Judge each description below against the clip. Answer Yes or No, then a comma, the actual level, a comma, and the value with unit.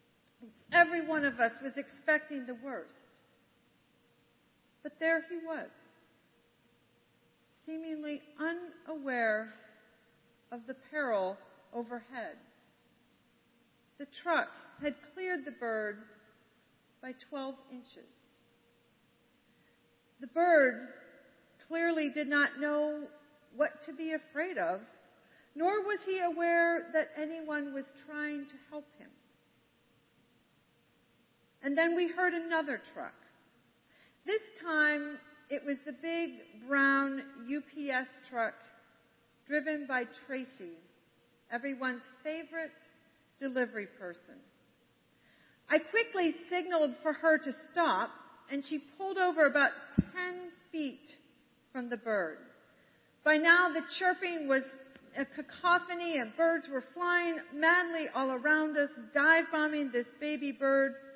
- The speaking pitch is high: Yes, very high, 295 Hz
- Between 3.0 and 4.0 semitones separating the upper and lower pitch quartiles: Yes, average, 3.7 semitones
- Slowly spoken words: Yes, slow, 105 wpm